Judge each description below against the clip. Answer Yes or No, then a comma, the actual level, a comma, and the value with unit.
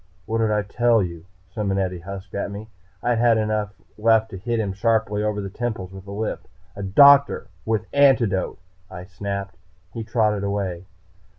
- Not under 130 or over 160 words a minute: No, average, 170 wpm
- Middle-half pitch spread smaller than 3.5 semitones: Yes, narrow, 2.4 semitones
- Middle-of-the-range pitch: No, low, 105 Hz